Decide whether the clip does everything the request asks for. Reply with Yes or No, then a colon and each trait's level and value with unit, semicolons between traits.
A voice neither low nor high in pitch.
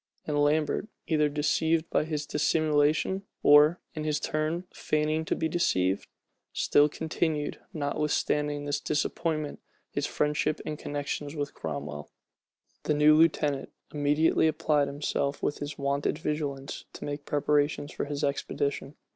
Yes: medium, 150 Hz